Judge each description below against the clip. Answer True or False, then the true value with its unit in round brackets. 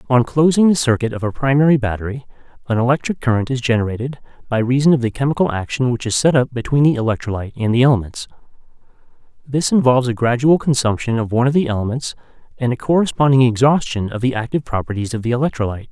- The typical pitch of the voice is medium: False (125 Hz)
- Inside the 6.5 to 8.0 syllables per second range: True (7.0 syllables/s)